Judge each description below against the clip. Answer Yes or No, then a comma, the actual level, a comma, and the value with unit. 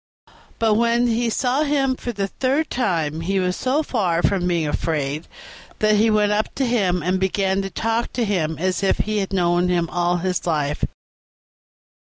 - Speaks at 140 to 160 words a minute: No, average, 185 wpm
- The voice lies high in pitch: Yes, high, 195 Hz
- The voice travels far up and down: No, average, 4.7 semitones